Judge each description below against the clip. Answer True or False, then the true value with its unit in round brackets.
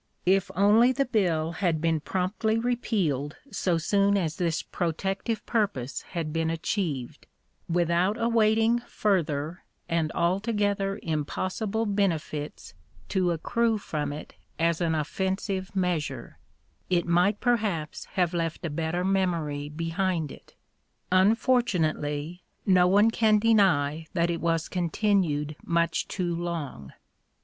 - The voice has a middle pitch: True (175 Hz)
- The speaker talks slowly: True (120 wpm)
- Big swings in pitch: False (4.0 semitones)